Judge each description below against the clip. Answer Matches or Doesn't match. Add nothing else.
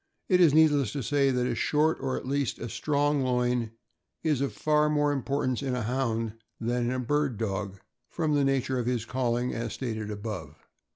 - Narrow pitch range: Doesn't match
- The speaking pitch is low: Matches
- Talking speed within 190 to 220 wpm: Matches